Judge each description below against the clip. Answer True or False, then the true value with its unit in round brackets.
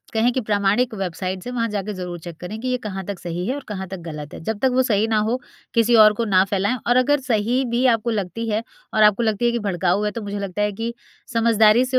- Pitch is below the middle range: False (215 Hz)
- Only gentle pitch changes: False (3.5 semitones)